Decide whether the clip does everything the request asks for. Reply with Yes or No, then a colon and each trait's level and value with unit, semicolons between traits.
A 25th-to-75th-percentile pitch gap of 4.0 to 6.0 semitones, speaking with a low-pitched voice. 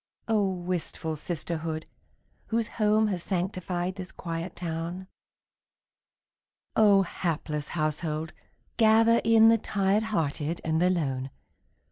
No: average, 4.4 semitones; medium, 180 Hz